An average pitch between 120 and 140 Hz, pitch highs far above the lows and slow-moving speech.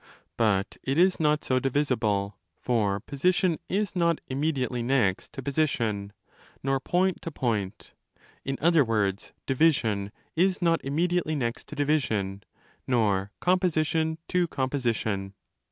Yes: low, 135 Hz; wide, 6.7 semitones; slow, 120 wpm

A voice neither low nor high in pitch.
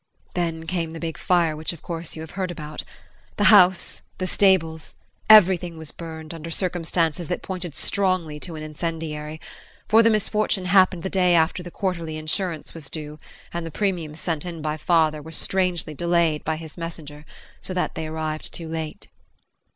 Yes: medium, 165 Hz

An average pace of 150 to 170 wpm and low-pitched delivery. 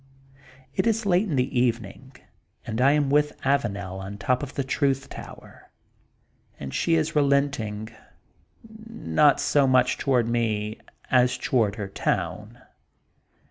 No: slow, 135 wpm; low, 125 Hz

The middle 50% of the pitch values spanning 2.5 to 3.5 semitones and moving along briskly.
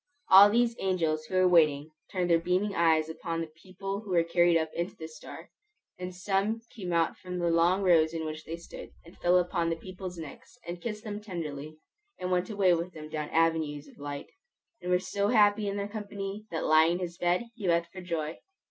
Yes: average, 2.9 semitones; fast, 215 wpm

